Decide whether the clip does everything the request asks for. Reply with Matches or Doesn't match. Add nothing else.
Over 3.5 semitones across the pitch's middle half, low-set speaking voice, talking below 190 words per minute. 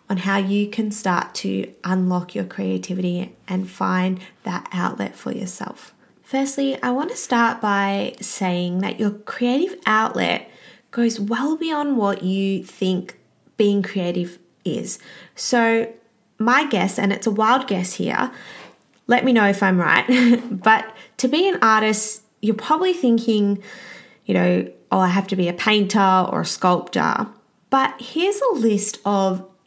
Doesn't match